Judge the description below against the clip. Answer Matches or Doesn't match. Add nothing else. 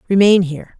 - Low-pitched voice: Doesn't match